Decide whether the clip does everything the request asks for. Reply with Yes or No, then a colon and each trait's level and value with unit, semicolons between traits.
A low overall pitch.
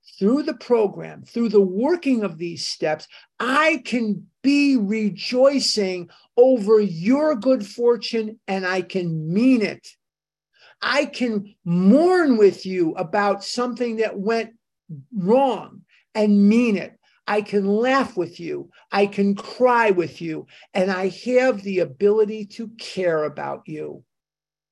No: high, 210 Hz